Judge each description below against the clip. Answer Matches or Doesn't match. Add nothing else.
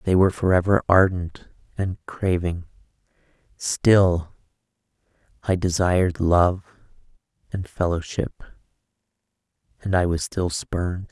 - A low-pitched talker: Matches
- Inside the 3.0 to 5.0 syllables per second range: Matches